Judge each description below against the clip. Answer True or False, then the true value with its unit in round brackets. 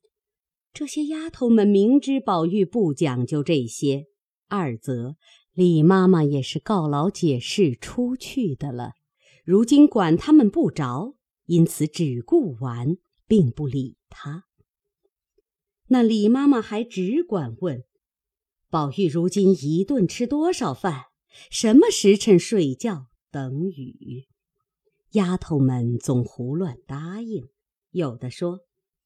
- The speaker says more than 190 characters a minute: False (170 characters per minute)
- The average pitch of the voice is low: False (180 Hz)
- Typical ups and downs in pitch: False (7.5 semitones)